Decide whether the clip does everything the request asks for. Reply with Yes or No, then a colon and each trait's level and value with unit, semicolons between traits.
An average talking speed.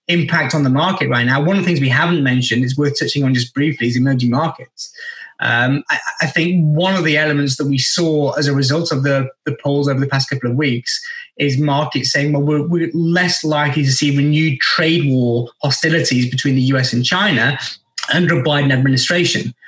No: fast, 210 wpm